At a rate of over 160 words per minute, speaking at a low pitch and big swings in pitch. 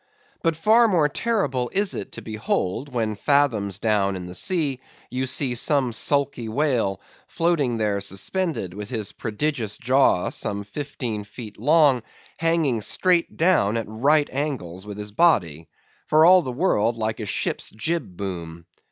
No: average, 150 wpm; low, 125 Hz; wide, 6.6 semitones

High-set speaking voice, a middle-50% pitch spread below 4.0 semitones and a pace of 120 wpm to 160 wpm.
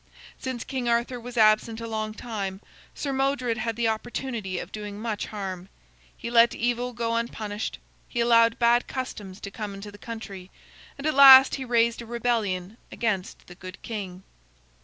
No: high, 230 Hz; average, 2.8 semitones; average, 170 wpm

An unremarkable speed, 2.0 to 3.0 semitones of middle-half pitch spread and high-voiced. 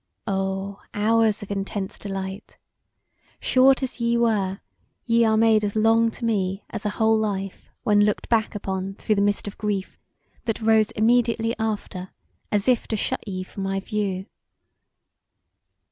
Yes: average, 155 wpm; narrow, 2.4 semitones; high, 210 Hz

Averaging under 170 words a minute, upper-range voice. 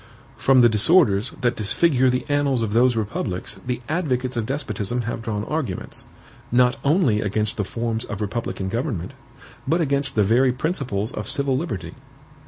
No: average, 160 wpm; low, 120 Hz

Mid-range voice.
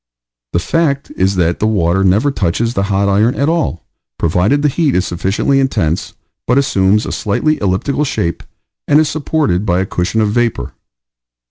No: low, 105 Hz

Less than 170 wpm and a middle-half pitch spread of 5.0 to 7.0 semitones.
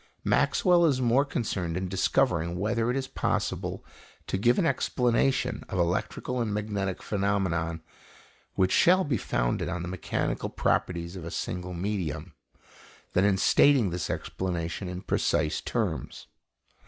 Yes: average, 140 wpm; wide, 5.4 semitones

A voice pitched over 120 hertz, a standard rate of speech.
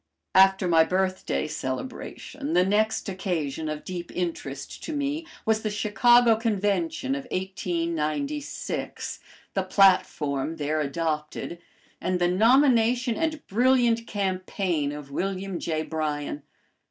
No: high, 190 Hz; slow, 115 wpm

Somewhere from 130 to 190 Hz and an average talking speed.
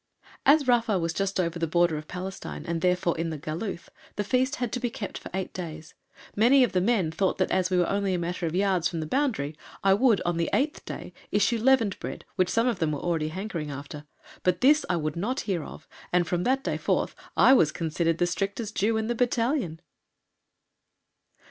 No: medium, 185 Hz; fast, 220 wpm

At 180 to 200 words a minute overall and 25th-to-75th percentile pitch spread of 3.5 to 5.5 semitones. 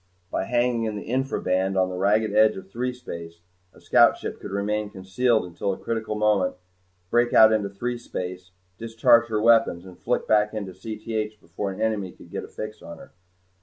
No: average, 185 wpm; average, 3.1 semitones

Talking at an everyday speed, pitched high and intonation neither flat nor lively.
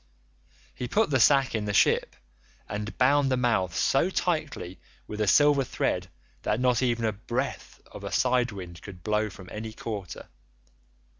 No: average, 165 wpm; low, 110 Hz; average, 4.3 semitones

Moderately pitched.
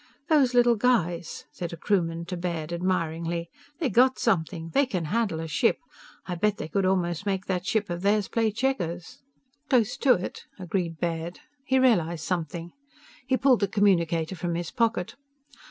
Yes: medium, 180 Hz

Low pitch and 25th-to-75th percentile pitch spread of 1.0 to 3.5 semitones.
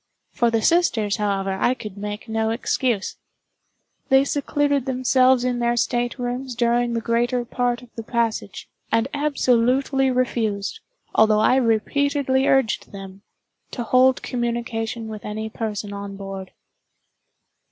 No: high, 235 Hz; average, 2.8 semitones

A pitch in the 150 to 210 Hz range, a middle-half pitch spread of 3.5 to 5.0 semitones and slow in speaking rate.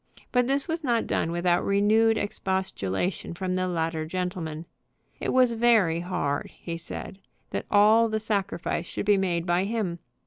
No: high, 190 Hz; average, 4.3 semitones; average, 160 wpm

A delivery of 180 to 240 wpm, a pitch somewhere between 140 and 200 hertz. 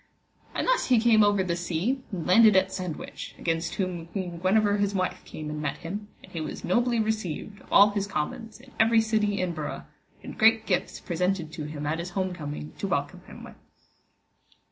Yes: average, 200 wpm; high, 190 Hz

